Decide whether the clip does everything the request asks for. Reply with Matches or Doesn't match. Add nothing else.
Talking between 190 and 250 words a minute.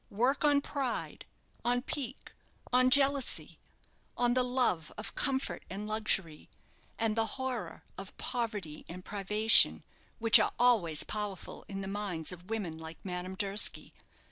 Doesn't match